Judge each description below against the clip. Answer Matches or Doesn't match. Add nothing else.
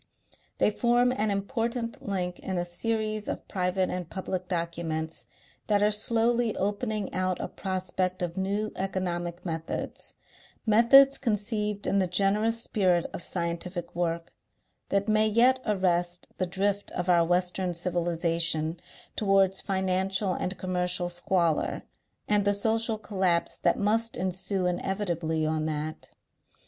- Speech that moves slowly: Matches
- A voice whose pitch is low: Doesn't match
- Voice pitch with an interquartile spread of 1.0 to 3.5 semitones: Matches